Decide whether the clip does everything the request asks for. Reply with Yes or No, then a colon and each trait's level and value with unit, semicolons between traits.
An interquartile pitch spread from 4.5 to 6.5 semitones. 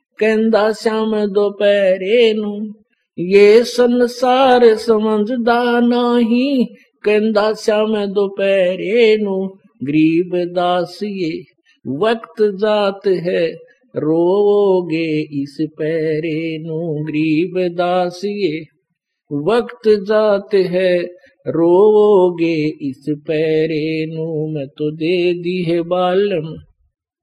Yes: average, 4.8 semitones